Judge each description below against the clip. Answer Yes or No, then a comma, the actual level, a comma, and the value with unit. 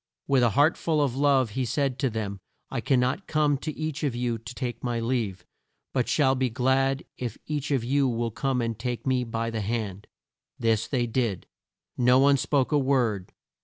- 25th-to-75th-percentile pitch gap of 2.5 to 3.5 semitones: Yes, average, 3.1 semitones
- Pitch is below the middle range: Yes, low, 125 Hz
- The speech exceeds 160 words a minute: Yes, average, 200 wpm